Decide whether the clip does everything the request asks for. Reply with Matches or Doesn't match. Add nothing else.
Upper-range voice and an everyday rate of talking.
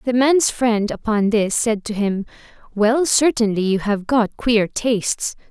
Matches